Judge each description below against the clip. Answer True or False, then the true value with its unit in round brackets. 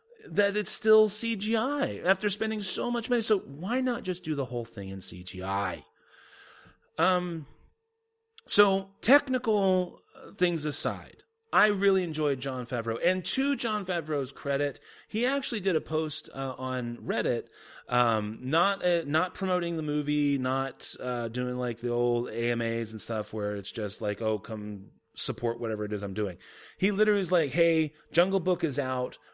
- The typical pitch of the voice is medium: True (155 Hz)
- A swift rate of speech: False (160 wpm)